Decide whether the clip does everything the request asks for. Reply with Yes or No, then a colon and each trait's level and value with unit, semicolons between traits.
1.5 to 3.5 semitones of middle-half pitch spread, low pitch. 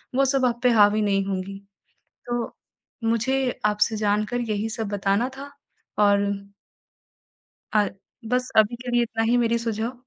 No: average, 2.8 semitones; high, 225 Hz